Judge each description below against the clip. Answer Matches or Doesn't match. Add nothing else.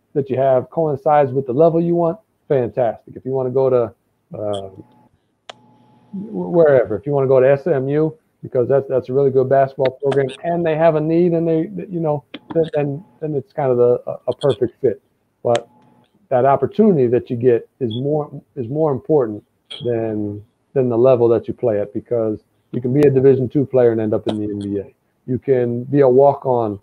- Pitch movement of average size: Matches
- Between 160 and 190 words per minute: Doesn't match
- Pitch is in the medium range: Doesn't match